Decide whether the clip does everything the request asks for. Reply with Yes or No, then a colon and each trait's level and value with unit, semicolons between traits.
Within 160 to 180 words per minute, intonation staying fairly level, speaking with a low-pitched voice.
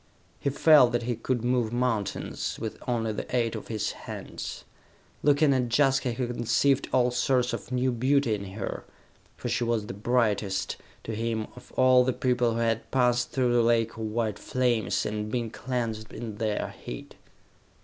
Yes: average, 175 wpm; narrow, 2.3 semitones; low, 120 Hz